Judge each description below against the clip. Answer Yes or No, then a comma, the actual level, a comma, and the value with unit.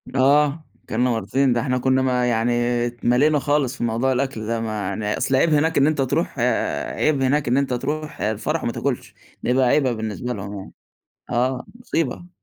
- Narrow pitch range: No, average, 3.3 semitones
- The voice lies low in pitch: Yes, low, 130 Hz